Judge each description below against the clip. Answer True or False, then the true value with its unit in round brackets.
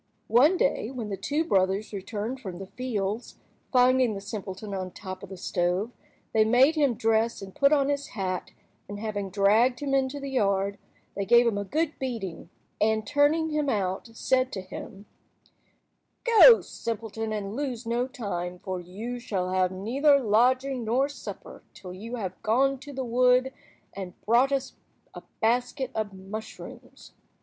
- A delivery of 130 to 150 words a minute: False (165 wpm)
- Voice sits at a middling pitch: False (225 Hz)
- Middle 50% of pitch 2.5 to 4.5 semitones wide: False (4.9 semitones)